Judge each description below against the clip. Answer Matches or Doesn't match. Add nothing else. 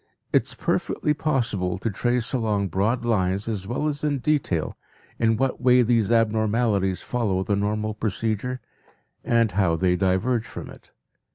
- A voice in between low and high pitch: Doesn't match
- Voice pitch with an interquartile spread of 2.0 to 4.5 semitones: Matches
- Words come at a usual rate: Matches